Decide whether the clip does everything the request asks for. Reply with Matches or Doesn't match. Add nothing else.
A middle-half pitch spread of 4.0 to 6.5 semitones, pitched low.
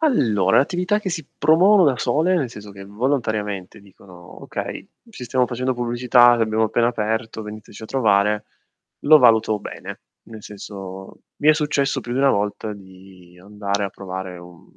Matches